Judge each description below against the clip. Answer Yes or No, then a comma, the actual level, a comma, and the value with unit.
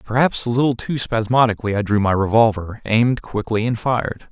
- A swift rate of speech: No, average, 180 wpm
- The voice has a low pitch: Yes, low, 115 Hz